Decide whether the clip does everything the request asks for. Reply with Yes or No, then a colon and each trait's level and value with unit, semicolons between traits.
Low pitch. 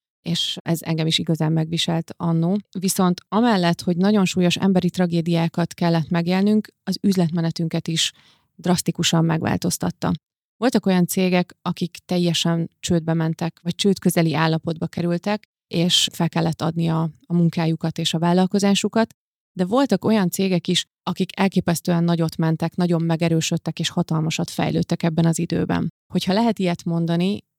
No: medium, 170 Hz